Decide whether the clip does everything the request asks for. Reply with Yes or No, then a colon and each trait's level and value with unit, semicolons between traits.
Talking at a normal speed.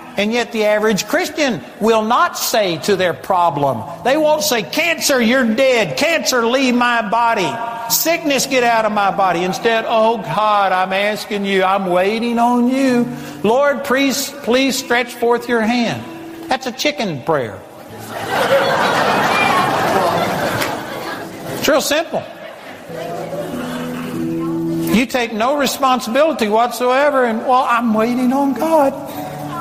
No: slow, 130 wpm